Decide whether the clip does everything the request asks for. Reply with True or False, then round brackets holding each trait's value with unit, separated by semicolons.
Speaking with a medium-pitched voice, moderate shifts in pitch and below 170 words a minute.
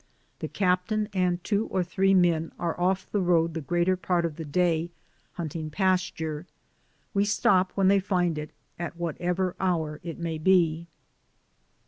False (175 Hz; 2.3 semitones; 160 wpm)